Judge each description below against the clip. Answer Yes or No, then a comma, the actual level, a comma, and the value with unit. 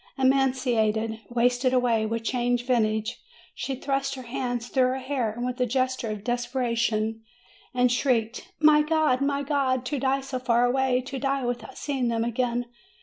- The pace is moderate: Yes, average, 160 wpm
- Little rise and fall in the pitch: Yes, narrow, 2.1 semitones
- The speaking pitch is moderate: No, very high, 250 Hz